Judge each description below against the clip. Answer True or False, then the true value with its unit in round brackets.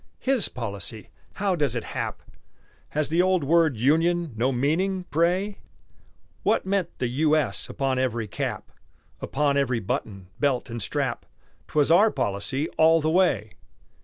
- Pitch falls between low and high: True (150 Hz)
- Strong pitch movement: True (5.9 semitones)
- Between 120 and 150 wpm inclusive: True (145 wpm)